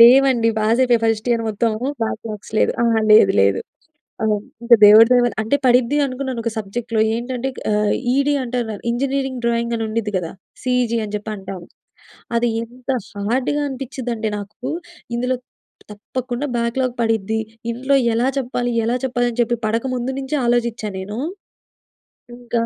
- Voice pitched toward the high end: Yes, high, 235 Hz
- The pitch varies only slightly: Yes, narrow, 2.3 semitones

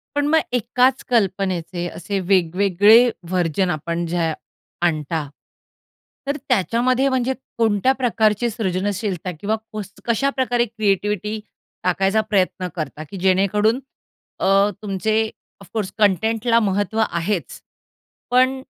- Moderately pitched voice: No, high, 205 Hz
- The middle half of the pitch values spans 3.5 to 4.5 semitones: Yes, average, 3.9 semitones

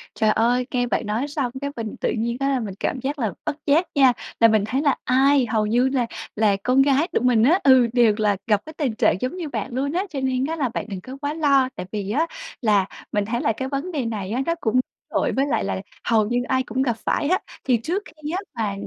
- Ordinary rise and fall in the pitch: Yes, average, 4.2 semitones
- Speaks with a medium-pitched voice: No, very high, 255 Hz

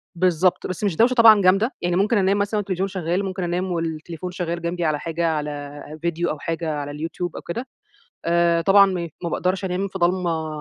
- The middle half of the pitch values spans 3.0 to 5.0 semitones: No, narrow, 2.5 semitones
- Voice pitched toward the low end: No, medium, 175 Hz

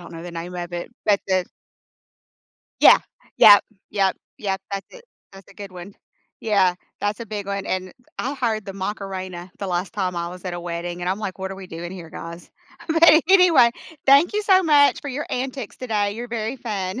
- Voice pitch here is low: No, high, 195 Hz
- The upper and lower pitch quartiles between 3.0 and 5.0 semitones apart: Yes, average, 4.6 semitones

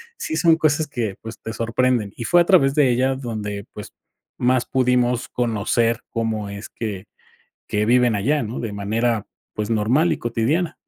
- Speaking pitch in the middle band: No, low, 120 Hz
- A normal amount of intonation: Yes, average, 3.5 semitones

